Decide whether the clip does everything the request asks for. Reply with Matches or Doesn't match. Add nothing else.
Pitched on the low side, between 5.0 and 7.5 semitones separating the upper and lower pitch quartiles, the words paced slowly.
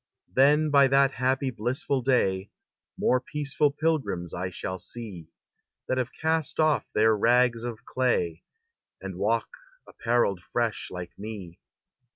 Matches